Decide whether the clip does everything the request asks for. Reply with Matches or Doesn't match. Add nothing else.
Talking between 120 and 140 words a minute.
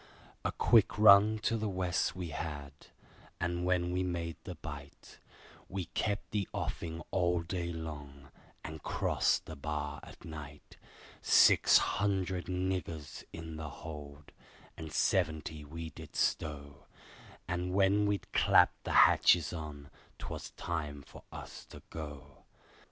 Matches